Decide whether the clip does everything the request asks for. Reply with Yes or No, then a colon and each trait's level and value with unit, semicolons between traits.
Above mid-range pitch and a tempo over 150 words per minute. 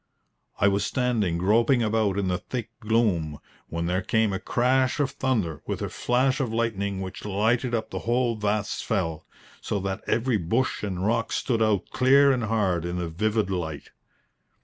No: low, 110 Hz; average, 175 wpm